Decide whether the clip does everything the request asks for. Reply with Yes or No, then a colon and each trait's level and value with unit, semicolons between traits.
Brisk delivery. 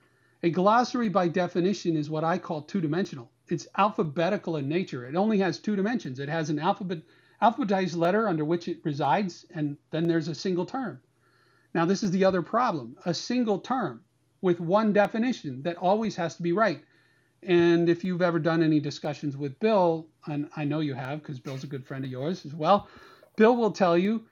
No: average, 195 wpm